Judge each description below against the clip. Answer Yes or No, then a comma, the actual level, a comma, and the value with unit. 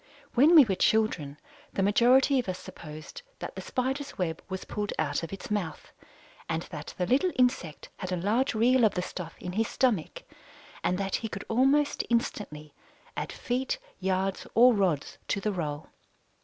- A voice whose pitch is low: No, high, 200 Hz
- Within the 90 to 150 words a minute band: No, average, 175 wpm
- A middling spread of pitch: No, wide, 5.9 semitones